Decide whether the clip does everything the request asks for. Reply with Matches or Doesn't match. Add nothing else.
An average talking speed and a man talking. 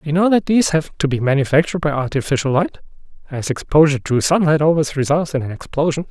Matches